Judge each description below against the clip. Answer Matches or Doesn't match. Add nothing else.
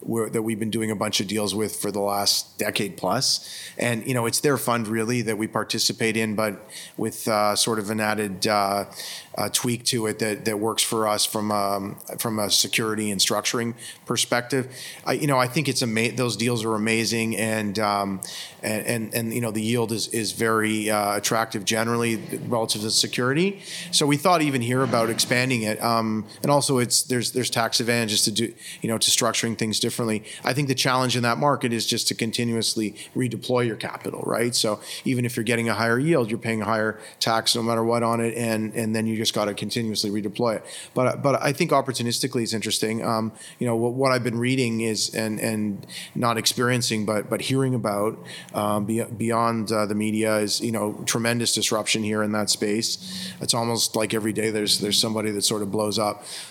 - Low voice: Matches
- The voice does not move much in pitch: Matches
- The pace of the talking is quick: Matches